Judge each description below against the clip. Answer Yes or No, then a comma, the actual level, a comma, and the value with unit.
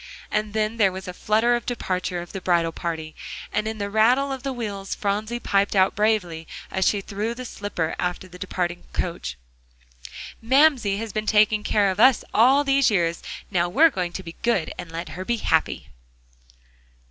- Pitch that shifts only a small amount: No, average, 4.1 semitones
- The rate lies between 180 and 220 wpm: Yes, average, 185 wpm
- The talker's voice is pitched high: Yes, high, 205 Hz